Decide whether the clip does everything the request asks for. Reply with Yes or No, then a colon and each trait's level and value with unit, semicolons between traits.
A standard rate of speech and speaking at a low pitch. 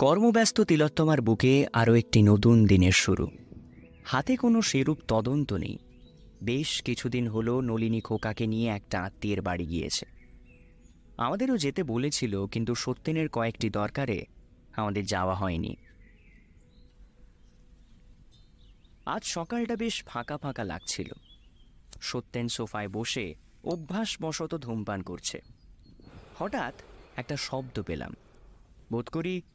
Yes: average, 105 wpm; low, 115 Hz